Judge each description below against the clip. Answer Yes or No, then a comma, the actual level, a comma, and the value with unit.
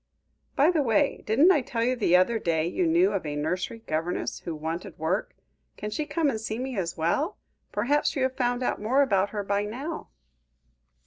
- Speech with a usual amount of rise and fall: No, wide, 7.1 semitones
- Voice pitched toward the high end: Yes, high, 220 Hz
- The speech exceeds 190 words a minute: Yes, average, 200 wpm